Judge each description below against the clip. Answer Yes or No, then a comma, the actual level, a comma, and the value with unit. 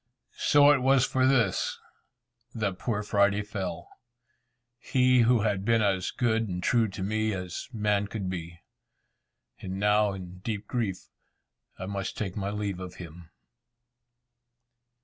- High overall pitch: No, low, 105 Hz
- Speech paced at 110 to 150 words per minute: Yes, average, 140 wpm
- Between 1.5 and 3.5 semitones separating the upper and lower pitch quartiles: Yes, average, 3.2 semitones